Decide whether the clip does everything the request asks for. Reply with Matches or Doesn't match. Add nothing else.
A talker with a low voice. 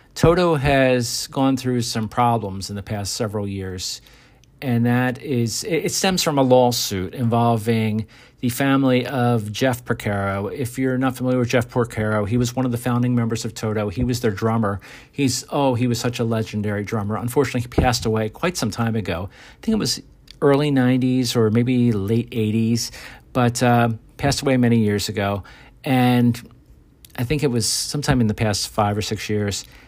Matches